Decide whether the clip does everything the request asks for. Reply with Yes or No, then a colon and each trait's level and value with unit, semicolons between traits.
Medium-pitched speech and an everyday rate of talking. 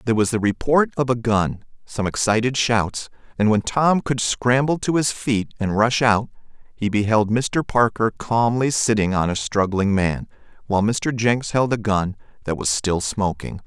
No: low, 110 Hz; average, 180 wpm